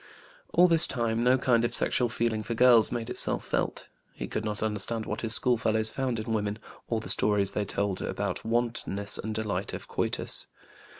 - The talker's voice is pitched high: No, low, 115 Hz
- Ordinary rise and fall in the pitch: No, narrow, 1.9 semitones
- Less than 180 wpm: No, average, 185 wpm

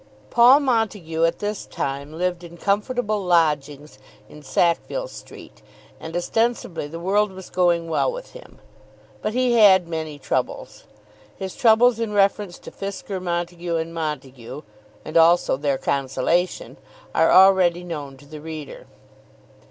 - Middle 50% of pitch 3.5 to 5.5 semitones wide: Yes, average, 4.7 semitones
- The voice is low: No, medium, 175 Hz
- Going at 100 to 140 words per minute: Yes, slow, 135 wpm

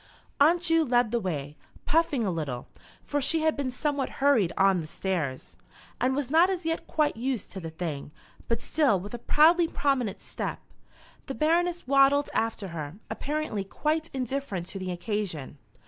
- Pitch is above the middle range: Yes, very high, 255 Hz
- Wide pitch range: Yes, wide, 8.2 semitones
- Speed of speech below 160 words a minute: No, average, 170 wpm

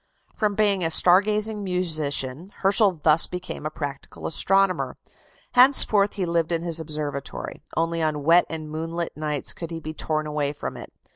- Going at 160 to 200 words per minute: Yes, average, 165 wpm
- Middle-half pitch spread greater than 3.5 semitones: Yes, average, 3.9 semitones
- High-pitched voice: No, medium, 165 Hz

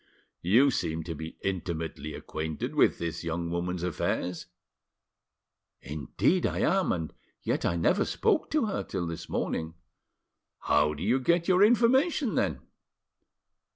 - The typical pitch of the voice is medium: No, very low, 90 Hz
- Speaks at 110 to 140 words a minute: Yes, slow, 135 wpm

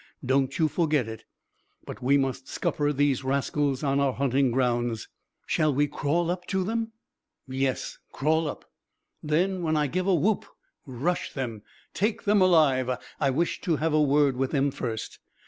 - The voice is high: No, medium, 145 Hz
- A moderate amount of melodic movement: Yes, average, 3.7 semitones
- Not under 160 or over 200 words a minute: Yes, average, 165 wpm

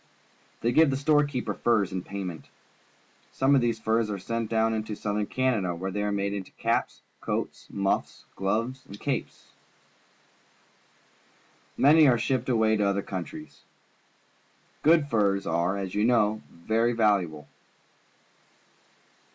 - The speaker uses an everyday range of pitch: Yes, average, 3.8 semitones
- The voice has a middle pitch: No, low, 110 Hz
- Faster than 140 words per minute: No, slow, 135 wpm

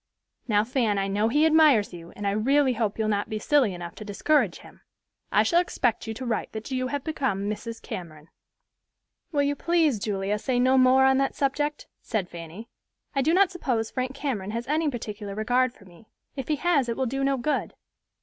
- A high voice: Yes, high, 245 Hz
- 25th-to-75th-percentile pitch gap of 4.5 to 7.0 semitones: Yes, average, 5.1 semitones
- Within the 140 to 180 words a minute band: No, fast, 205 wpm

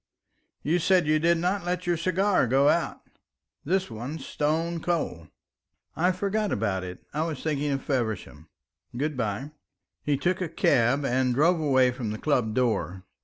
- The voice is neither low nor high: Yes, medium, 145 Hz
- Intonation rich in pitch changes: Yes, wide, 5.7 semitones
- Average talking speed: Yes, average, 170 wpm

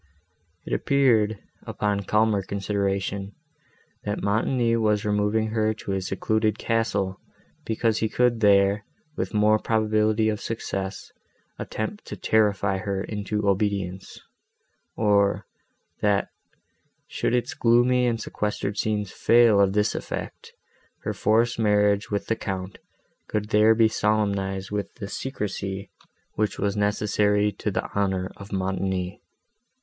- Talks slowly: Yes, slow, 125 wpm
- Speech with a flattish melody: Yes, narrow, 1.6 semitones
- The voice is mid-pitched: No, low, 105 Hz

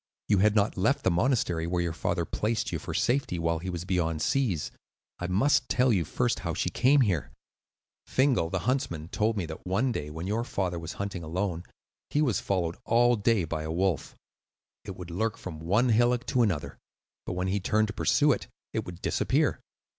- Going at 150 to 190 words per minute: No, average, 200 wpm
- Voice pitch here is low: Yes, very low, 95 Hz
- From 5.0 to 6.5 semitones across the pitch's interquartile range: Yes, wide, 5.4 semitones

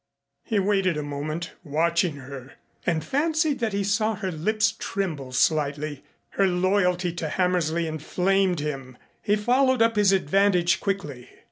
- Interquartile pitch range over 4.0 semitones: Yes, average, 4.8 semitones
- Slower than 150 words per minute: Yes, average, 140 wpm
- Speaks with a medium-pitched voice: Yes, medium, 180 Hz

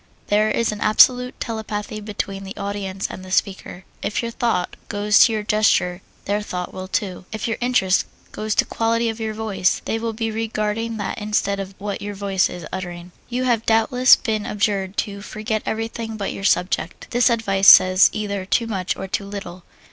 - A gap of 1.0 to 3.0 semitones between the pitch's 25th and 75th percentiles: Yes, narrow, 2.4 semitones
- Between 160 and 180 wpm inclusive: No, average, 195 wpm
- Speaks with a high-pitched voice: Yes, high, 210 Hz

